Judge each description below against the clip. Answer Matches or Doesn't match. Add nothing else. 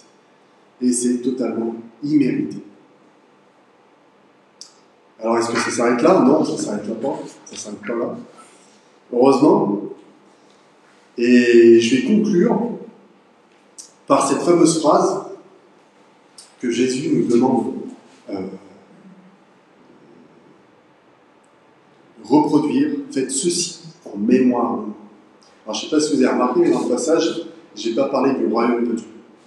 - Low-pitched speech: Matches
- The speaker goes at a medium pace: Doesn't match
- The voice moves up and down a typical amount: Doesn't match